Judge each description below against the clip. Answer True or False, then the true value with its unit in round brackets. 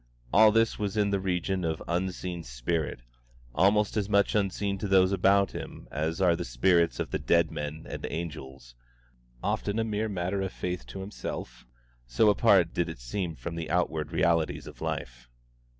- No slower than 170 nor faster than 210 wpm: True (175 wpm)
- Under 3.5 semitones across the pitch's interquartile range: False (3.8 semitones)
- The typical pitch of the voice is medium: False (90 Hz)